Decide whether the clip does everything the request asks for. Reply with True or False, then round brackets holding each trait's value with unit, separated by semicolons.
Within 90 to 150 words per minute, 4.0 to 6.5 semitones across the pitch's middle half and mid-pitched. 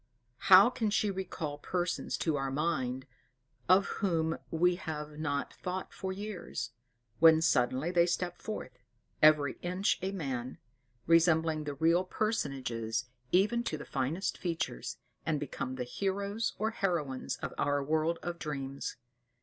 True (140 wpm; 4.5 semitones; 160 Hz)